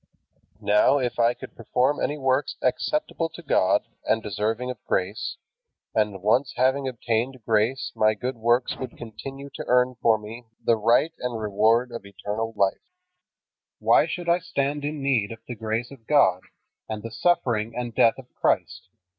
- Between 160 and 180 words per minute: Yes, average, 165 wpm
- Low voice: Yes, low, 120 Hz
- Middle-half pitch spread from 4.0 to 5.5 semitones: No, average, 3.4 semitones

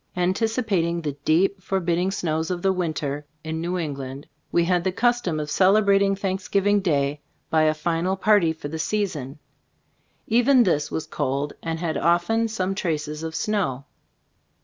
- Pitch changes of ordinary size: Yes, average, 4.0 semitones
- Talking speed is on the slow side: No, average, 155 wpm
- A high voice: No, medium, 175 Hz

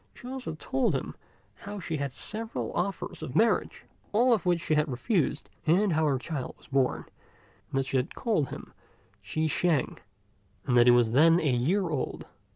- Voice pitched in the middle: Yes, medium, 155 Hz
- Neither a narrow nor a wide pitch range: No, wide, 6.6 semitones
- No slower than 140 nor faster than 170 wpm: No, average, 190 wpm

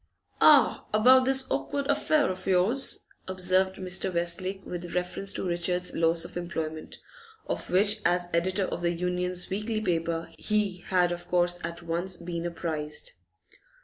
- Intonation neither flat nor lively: No, narrow, 2.0 semitones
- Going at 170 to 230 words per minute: No, average, 150 wpm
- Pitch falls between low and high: Yes, medium, 180 Hz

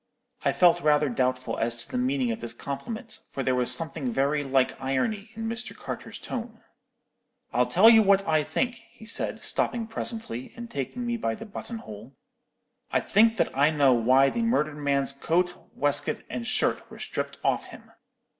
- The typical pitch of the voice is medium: Yes, medium, 145 Hz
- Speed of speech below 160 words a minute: No, average, 185 wpm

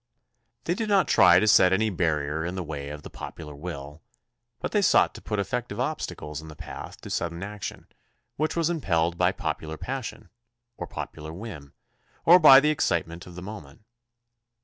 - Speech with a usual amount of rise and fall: No, wide, 7.6 semitones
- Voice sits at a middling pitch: No, very low, 90 Hz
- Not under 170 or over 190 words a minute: Yes, average, 180 wpm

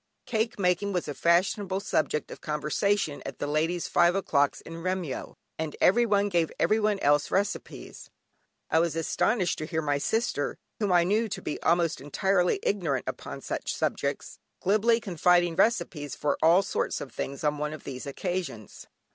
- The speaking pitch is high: No, medium, 175 Hz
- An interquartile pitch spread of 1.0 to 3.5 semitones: No, average, 4.7 semitones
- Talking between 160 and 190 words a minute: Yes, average, 165 wpm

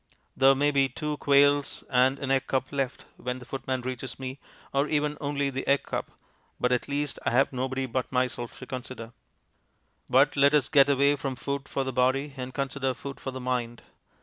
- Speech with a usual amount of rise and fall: No, narrow, 1.6 semitones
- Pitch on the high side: No, low, 135 Hz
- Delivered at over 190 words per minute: Yes, average, 200 wpm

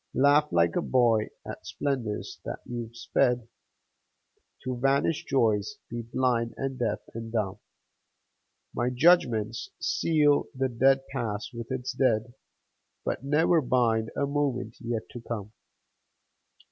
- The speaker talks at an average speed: No, slow, 125 wpm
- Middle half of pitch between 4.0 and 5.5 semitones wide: No, average, 3.1 semitones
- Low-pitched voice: Yes, low, 120 Hz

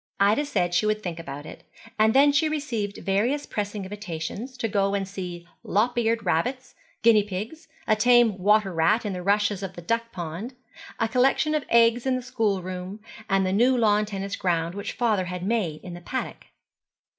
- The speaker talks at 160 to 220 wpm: Yes, average, 190 wpm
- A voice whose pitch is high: Yes, high, 210 Hz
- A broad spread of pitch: No, average, 3.9 semitones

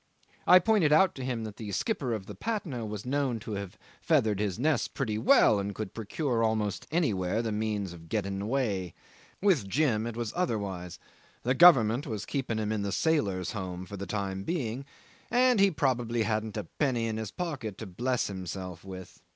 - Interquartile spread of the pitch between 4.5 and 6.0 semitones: Yes, average, 5.2 semitones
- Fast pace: No, average, 190 wpm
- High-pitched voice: No, low, 110 Hz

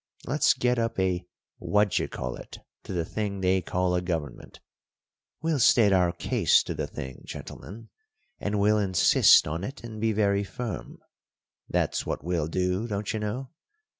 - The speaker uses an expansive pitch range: No, average, 3.6 semitones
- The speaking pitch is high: No, low, 100 Hz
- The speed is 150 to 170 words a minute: Yes, average, 165 wpm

